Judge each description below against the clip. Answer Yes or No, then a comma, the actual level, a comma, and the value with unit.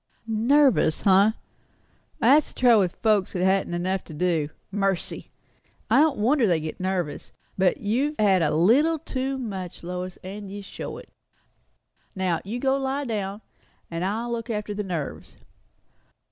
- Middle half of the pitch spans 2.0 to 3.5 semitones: No, average, 4.7 semitones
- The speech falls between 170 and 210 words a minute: No, average, 155 wpm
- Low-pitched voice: No, high, 200 Hz